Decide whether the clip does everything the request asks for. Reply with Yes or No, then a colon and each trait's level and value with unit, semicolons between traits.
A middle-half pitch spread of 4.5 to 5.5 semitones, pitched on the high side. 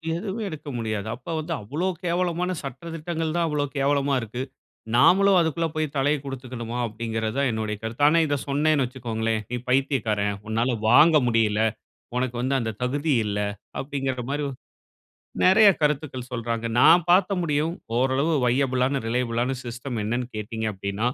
No: average, 4.9 semitones; low, 130 Hz